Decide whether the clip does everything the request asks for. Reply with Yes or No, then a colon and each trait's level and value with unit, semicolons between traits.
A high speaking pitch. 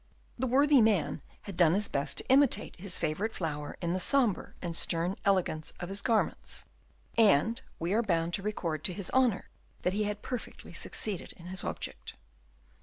Yes: high, 195 Hz